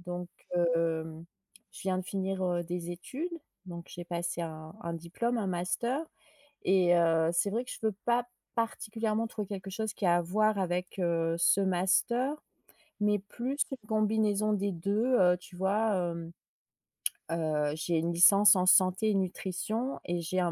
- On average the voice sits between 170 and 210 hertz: Yes, medium, 185 Hz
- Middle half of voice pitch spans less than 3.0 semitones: No, average, 3.8 semitones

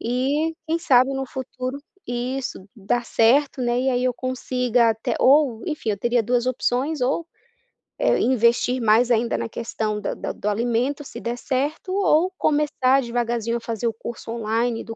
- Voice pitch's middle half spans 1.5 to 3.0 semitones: Yes, narrow, 2.5 semitones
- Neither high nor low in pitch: No, high, 245 Hz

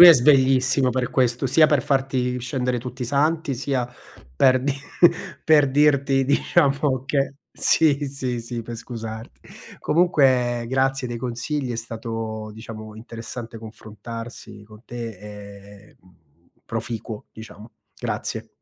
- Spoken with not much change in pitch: No, average, 3.2 semitones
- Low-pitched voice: Yes, low, 125 Hz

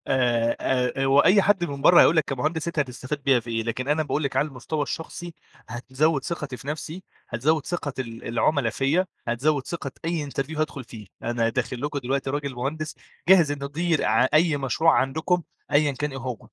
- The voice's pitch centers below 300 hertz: Yes, medium, 140 Hz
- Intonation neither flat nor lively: Yes, average, 3.6 semitones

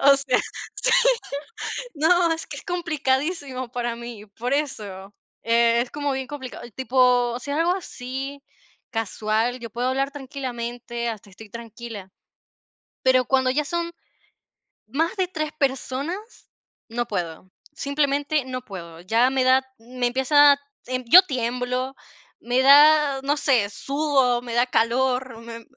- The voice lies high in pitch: Yes, very high, 255 Hz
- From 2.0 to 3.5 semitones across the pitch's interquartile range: Yes, average, 3.2 semitones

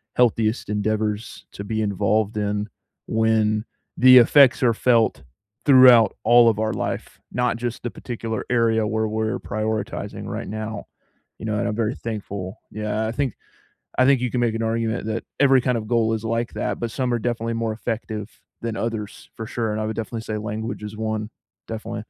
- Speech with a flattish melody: Yes, narrow, 1.5 semitones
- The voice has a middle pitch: No, low, 110 Hz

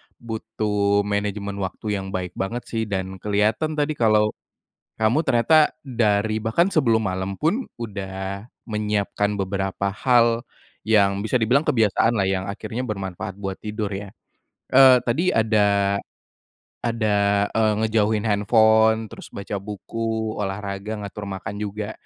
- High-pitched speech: No, low, 105 Hz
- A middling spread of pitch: No, narrow, 2.1 semitones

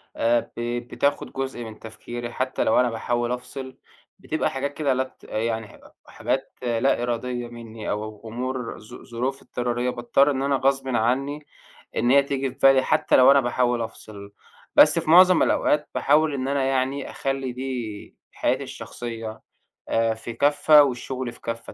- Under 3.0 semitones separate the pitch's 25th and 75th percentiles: Yes, narrow, 2.6 semitones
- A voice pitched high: No, low, 125 Hz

